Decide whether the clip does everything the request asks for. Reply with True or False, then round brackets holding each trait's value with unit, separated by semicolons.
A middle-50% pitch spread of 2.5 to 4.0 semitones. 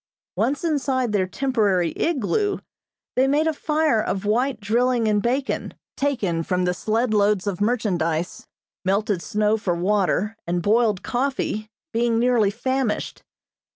False (4.5 semitones)